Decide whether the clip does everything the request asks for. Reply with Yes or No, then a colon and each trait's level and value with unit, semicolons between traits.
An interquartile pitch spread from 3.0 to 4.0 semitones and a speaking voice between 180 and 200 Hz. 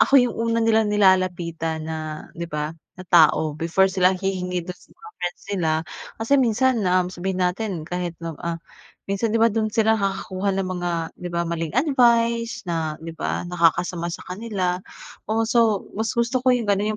No: average, 4.6 semitones; medium, 185 Hz